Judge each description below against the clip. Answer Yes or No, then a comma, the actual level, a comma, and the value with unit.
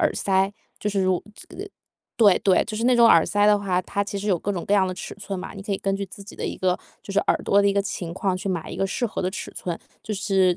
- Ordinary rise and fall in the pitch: No, narrow, 1.6 semitones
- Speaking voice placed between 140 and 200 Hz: Yes, high, 195 Hz